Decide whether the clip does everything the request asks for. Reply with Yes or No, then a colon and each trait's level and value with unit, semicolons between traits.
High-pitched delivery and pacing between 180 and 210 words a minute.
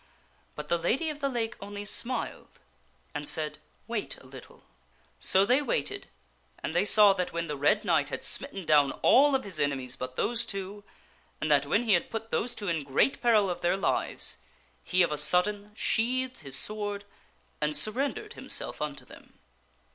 Yes: high, 200 Hz; average, 185 wpm